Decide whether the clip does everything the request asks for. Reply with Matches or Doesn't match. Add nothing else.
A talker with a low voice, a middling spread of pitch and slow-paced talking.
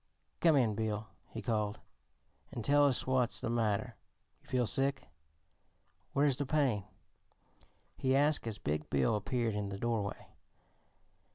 Matches